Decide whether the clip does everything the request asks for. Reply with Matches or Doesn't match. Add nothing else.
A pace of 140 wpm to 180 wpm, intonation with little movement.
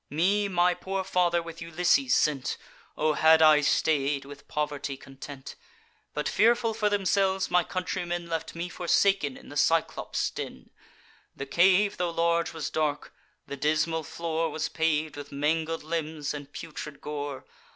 Doesn't match